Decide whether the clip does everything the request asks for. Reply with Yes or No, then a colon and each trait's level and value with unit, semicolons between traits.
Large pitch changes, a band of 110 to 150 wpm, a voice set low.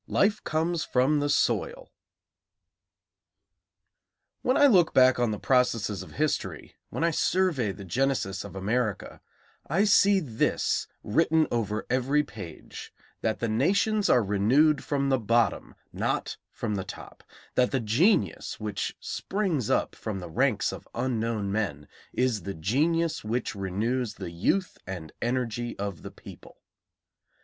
Yes: wide, 6.8 semitones; average, 140 wpm; low, 120 Hz